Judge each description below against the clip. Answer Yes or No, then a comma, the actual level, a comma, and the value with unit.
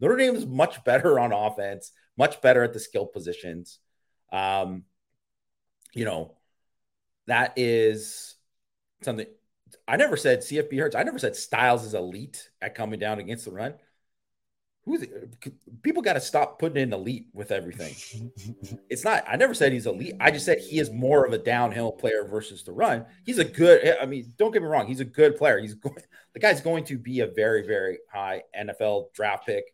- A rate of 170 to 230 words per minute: Yes, average, 190 wpm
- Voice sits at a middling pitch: No, low, 125 Hz